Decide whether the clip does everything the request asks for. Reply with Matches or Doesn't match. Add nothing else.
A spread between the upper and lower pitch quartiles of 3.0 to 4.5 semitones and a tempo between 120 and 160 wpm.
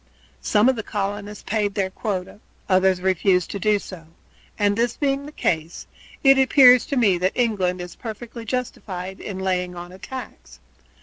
Doesn't match